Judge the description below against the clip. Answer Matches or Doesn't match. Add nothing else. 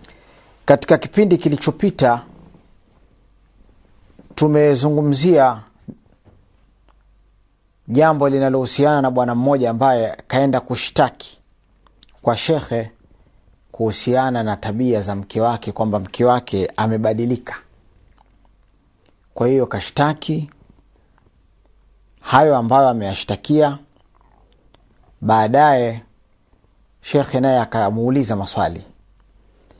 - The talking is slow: Matches